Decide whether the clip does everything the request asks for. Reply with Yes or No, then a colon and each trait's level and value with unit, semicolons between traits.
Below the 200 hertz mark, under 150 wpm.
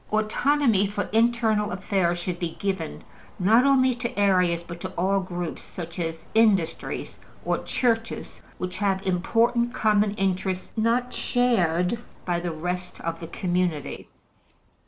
Yes: high, 190 Hz; slow, 135 wpm